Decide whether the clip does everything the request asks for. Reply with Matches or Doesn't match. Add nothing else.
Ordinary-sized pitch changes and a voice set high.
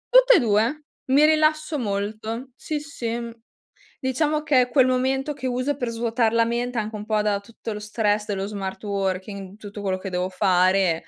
Matches